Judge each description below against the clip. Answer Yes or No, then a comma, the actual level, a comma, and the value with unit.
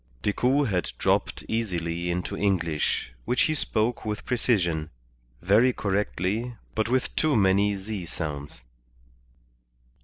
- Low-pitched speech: Yes, low, 100 Hz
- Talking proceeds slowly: Yes, slow, 115 wpm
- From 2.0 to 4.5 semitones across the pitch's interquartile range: No, average, 5.0 semitones